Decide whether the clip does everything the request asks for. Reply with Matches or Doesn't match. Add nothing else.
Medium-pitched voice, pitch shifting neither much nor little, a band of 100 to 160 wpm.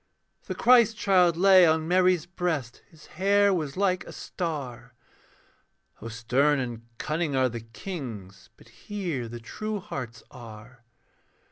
Doesn't match